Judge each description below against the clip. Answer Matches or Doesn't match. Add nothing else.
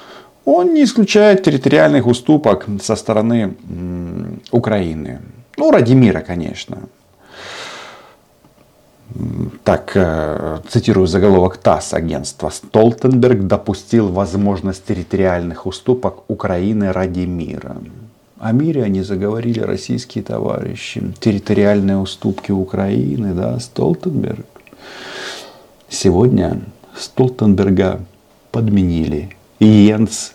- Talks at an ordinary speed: Doesn't match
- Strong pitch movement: Doesn't match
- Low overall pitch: Matches